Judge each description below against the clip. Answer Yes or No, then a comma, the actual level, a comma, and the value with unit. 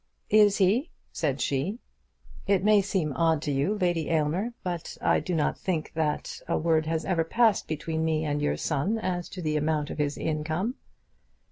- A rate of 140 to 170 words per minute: No, average, 180 wpm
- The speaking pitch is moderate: Yes, medium, 165 Hz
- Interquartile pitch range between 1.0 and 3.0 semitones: No, average, 4.0 semitones